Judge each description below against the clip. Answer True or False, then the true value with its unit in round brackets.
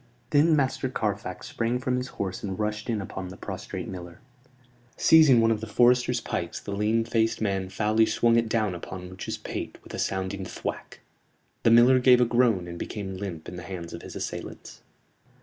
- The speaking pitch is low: True (105 Hz)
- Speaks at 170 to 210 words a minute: True (190 wpm)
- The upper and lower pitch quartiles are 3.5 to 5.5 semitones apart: True (4.1 semitones)